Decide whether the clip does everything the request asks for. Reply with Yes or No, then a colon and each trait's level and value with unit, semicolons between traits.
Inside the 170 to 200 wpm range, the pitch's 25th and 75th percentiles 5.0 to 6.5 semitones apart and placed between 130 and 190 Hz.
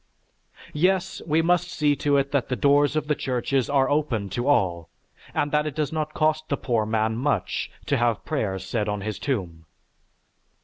Yes: average, 185 wpm; wide, 5.6 semitones; medium, 140 Hz